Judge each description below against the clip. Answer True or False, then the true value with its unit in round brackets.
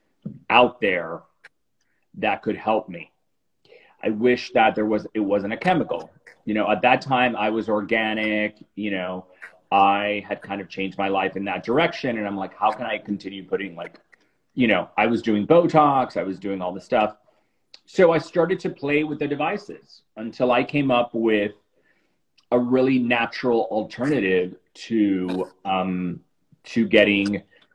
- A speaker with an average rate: True (165 wpm)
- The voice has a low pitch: True (110 Hz)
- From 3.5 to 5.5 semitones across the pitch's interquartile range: True (4.2 semitones)